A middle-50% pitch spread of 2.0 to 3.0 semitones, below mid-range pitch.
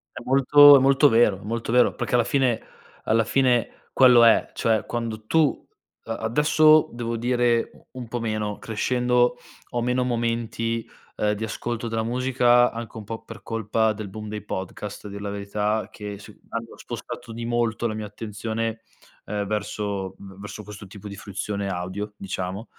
Yes: narrow, 2.5 semitones; low, 115 Hz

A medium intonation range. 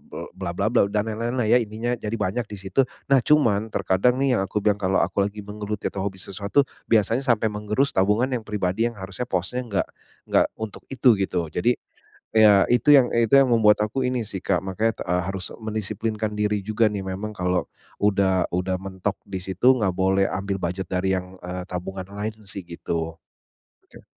Yes: average, 3.0 semitones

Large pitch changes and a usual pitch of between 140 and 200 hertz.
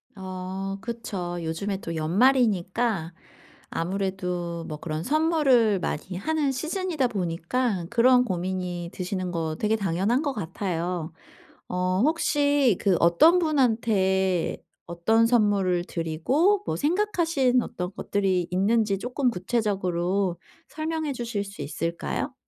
Yes: wide, 5.9 semitones; high, 195 Hz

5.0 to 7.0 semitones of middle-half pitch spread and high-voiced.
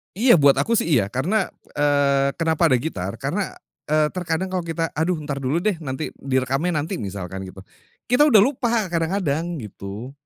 No: wide, 5.6 semitones; medium, 155 Hz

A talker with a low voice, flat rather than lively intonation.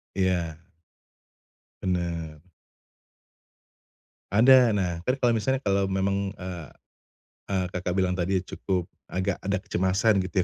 Yes: very low, 95 Hz; narrow, 1.8 semitones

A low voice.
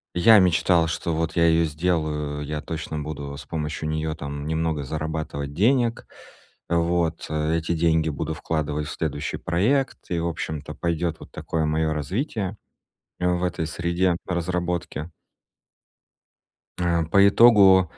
Yes: very low, 80 Hz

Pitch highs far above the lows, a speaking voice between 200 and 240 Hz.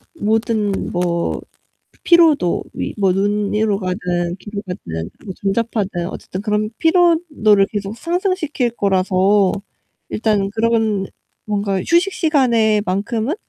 No: average, 3.4 semitones; high, 210 Hz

